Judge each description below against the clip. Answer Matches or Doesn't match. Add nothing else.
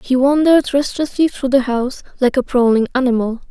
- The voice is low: Doesn't match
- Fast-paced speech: Doesn't match